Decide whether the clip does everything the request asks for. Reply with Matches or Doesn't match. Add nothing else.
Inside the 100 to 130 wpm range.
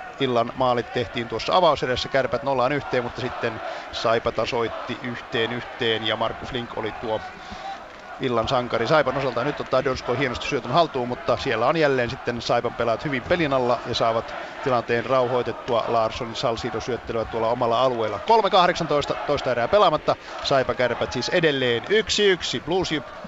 Doesn't match